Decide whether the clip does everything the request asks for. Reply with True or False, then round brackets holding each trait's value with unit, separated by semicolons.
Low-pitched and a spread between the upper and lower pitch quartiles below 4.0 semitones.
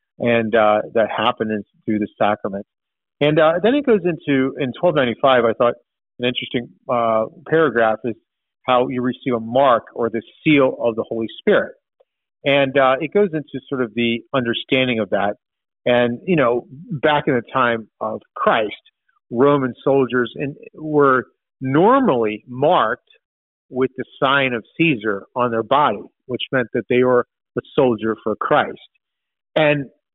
True (125 Hz; 3.6 semitones)